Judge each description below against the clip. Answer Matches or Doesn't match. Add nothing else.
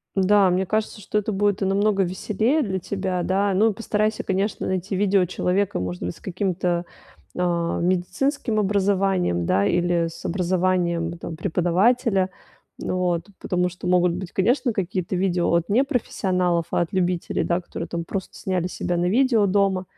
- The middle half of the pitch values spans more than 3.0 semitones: Doesn't match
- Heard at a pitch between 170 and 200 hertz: Matches